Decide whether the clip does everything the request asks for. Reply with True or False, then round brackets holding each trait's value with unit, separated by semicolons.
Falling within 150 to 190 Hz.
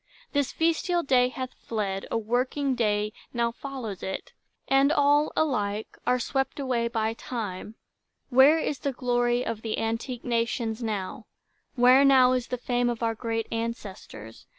False (240 Hz)